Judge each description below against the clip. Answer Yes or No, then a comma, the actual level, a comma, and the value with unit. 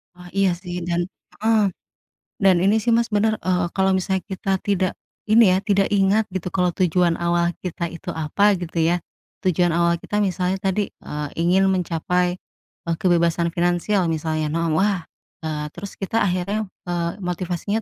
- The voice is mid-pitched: Yes, medium, 180 Hz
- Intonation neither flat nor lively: No, narrow, 2.3 semitones